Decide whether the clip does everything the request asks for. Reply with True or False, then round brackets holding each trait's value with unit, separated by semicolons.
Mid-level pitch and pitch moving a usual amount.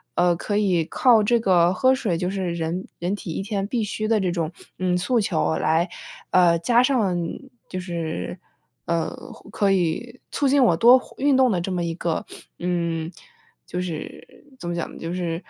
True (180 Hz; 4.1 semitones)